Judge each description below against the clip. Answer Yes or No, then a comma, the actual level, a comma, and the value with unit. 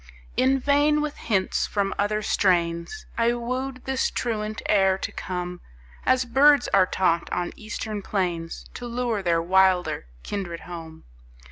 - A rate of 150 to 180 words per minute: No, average, 140 wpm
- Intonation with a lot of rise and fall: Yes, wide, 5.7 semitones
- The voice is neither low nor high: No, high, 205 Hz